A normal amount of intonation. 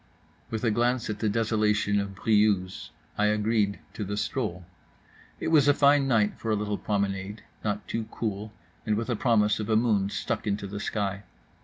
No: narrow, 1.8 semitones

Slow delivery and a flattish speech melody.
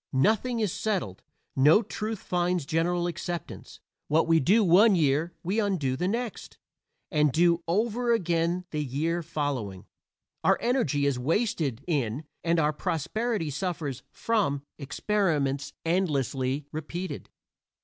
No: slow, 125 wpm; average, 5.2 semitones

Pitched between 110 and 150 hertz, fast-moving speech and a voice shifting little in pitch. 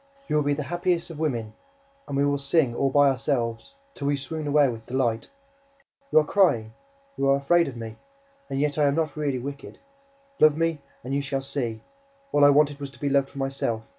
Yes: medium, 140 Hz; fast, 215 wpm; narrow, 2.0 semitones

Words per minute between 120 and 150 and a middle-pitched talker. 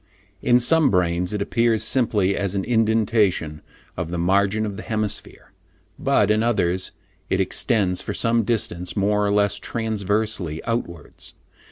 No: average, 145 wpm; low, 105 Hz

